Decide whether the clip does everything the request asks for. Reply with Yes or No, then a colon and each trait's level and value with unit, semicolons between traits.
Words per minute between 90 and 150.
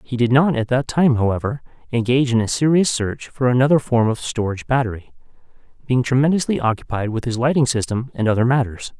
No: average, 185 wpm